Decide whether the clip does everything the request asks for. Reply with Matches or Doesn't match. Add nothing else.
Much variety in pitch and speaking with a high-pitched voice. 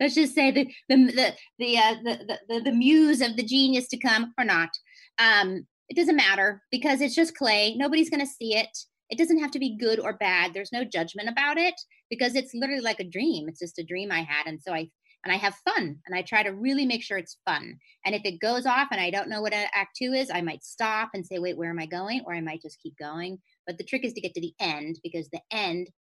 Matches